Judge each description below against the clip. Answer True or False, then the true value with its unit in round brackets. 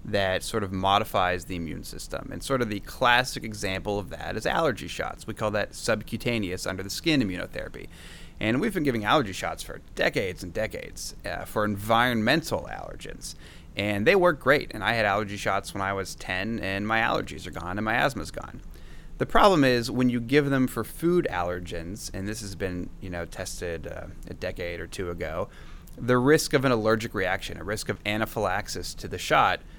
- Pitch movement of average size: True (3.7 semitones)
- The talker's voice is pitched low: True (105 Hz)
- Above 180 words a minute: True (195 wpm)